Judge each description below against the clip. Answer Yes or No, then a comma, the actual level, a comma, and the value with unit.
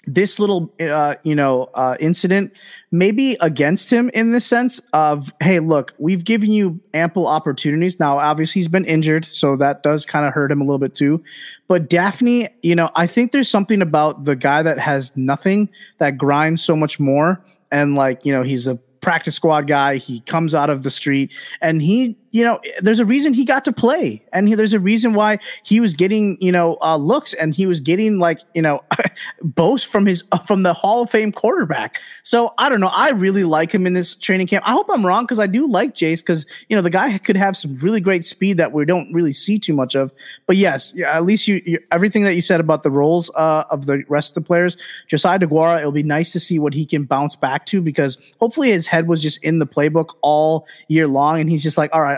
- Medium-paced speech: No, fast, 235 wpm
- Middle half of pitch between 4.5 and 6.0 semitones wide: Yes, average, 4.9 semitones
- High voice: No, medium, 170 Hz